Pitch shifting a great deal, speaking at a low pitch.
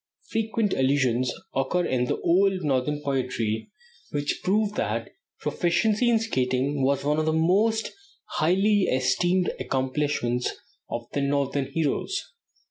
No: wide, 6.4 semitones; medium, 150 Hz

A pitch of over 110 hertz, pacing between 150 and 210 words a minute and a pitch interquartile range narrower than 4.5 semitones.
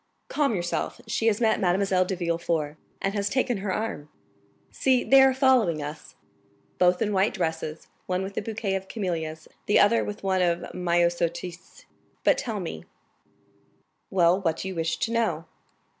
Yes: medium, 185 Hz; average, 165 wpm; average, 3.7 semitones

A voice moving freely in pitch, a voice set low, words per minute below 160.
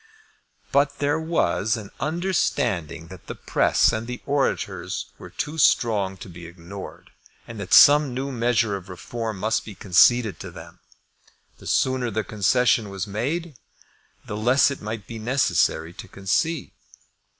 Yes: wide, 5.7 semitones; low, 115 Hz; average, 150 wpm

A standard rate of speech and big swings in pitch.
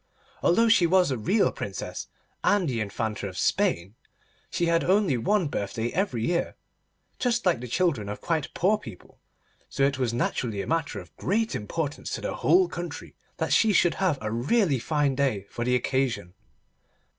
Yes: average, 175 wpm; wide, 8.1 semitones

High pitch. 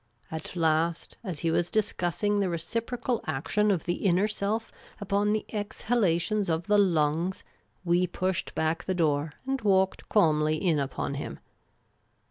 No: medium, 180 Hz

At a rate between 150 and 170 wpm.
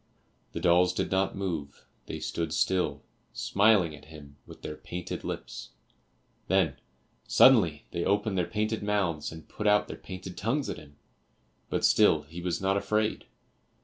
Yes: average, 155 wpm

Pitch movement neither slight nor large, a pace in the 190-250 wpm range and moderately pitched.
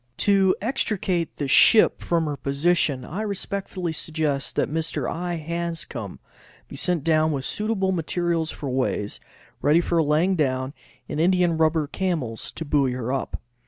No: average, 3.8 semitones; average, 150 wpm; medium, 160 Hz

